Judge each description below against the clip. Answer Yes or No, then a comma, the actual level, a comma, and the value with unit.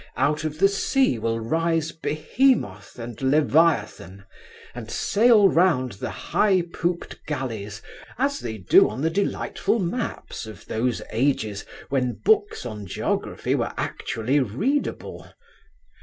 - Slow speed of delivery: Yes, slow, 125 wpm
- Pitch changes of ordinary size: No, wide, 8.1 semitones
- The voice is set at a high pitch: No, medium, 140 Hz